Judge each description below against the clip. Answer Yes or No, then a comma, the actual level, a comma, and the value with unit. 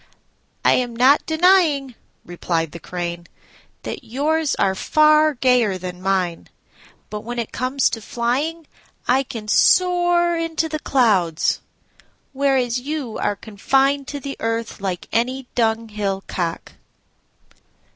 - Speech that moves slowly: Yes, slow, 125 wpm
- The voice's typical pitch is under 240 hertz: No, high, 245 Hz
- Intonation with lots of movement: Yes, wide, 6.1 semitones